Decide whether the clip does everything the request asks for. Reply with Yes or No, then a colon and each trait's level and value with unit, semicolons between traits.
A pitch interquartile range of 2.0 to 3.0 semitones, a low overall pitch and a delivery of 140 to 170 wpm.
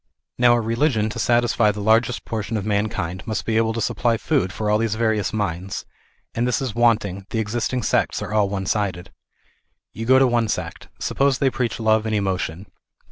No: narrow, 2.4 semitones; low, 110 Hz; average, 200 wpm